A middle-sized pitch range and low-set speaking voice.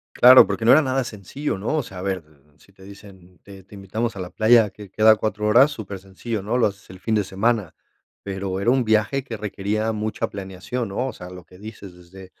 Yes: average, 3.0 semitones; low, 105 Hz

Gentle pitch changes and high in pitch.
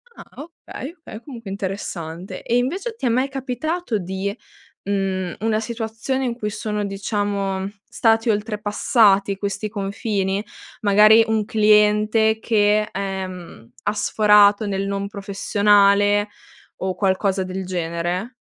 Yes: narrow, 2.3 semitones; high, 205 Hz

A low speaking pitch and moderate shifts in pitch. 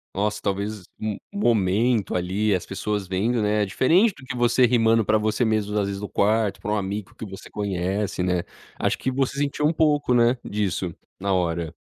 Yes: low, 105 Hz; average, 3.5 semitones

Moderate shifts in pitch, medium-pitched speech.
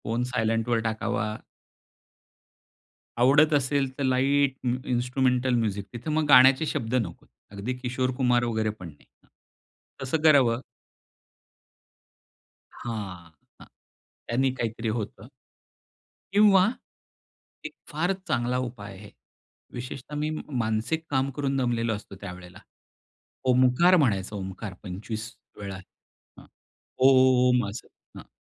No: average, 3.4 semitones; low, 125 Hz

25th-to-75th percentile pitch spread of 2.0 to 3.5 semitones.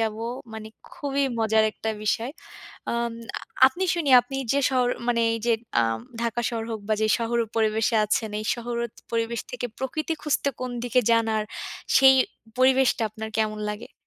Yes: average, 2.7 semitones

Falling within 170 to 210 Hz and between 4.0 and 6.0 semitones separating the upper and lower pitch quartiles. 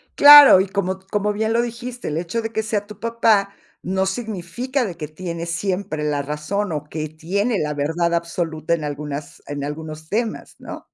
Yes: medium, 185 Hz; wide, 5.6 semitones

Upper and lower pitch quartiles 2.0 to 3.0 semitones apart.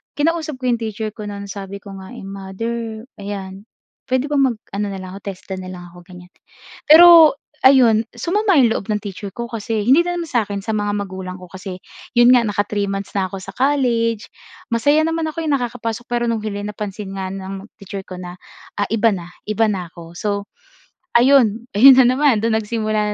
No: average, 3.7 semitones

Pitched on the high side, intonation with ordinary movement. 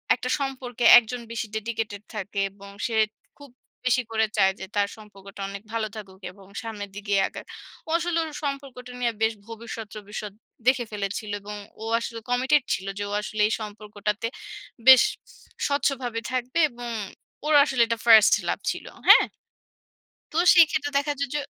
Yes: high, 230 Hz; average, 3.6 semitones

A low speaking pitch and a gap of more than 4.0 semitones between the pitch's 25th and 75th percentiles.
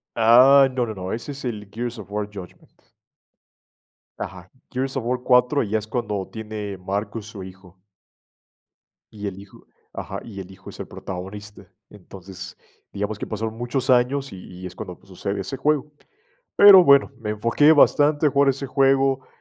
Yes: low, 110 Hz; average, 5.3 semitones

